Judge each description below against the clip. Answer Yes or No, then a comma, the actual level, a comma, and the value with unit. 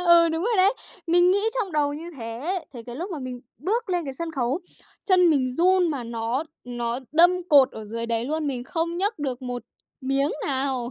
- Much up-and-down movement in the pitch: Yes, wide, 5.8 semitones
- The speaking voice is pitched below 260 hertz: No, very high, 290 Hz